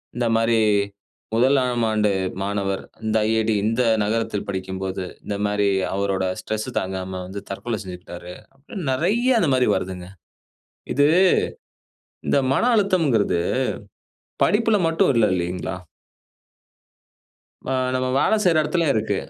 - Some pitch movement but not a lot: No, wide, 5.9 semitones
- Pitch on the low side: Yes, low, 110 Hz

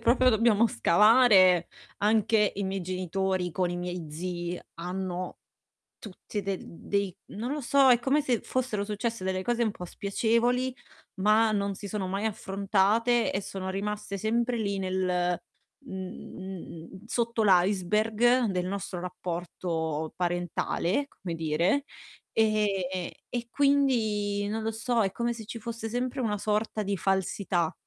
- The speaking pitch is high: Yes, high, 200 Hz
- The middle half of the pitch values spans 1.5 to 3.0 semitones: No, average, 3.7 semitones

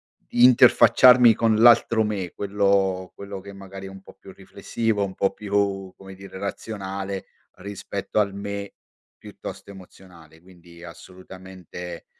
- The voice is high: No, very low, 95 Hz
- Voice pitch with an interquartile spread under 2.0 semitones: Yes, narrow, 1.4 semitones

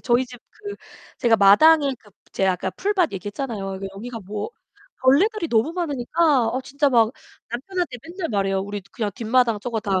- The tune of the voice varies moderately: No, wide, 6.8 semitones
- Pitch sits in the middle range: No, high, 240 Hz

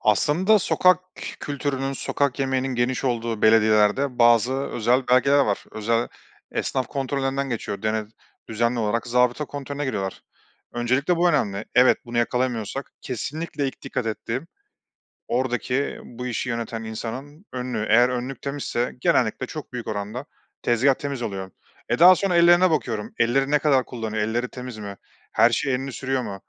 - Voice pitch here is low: Yes, low, 125 Hz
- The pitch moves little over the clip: No, average, 3.3 semitones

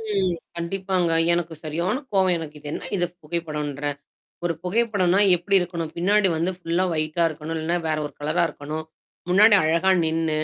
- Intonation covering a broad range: No, average, 2.8 semitones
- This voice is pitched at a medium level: Yes, medium, 170 Hz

